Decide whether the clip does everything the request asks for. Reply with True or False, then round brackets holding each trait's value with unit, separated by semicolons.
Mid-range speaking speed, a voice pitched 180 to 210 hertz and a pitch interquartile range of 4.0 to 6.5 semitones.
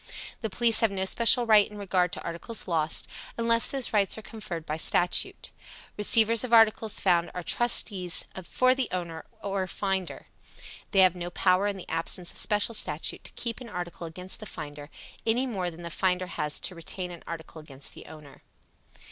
True (185 wpm; 185 Hz; 4.6 semitones)